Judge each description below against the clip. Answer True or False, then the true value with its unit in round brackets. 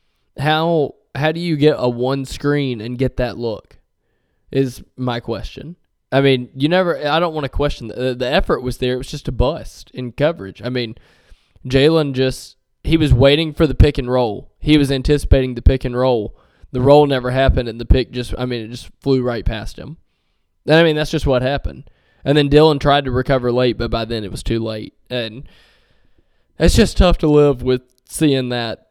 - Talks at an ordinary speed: False (210 wpm)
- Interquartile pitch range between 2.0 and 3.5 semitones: True (3.1 semitones)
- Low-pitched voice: True (130 Hz)